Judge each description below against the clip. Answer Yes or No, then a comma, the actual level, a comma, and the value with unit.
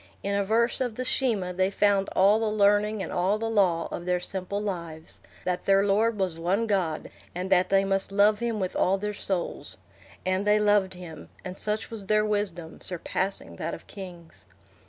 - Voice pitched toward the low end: No, high, 195 Hz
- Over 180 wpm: Yes, average, 190 wpm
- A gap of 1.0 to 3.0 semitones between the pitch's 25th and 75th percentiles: Yes, narrow, 2.6 semitones